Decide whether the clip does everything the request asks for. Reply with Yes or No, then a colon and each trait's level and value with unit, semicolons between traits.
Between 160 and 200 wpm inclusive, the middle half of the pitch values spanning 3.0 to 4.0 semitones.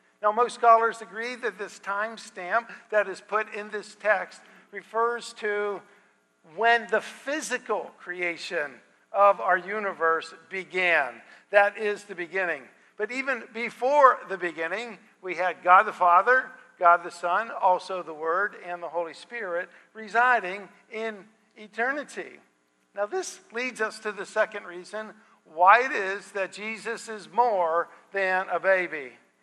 No: average, 140 wpm; average, 3.7 semitones